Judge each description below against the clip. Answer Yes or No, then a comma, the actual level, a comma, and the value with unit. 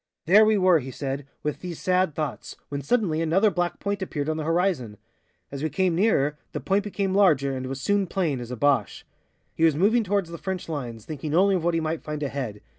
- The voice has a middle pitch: Yes, medium, 165 Hz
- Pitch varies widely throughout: No, average, 5.0 semitones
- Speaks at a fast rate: Yes, fast, 225 wpm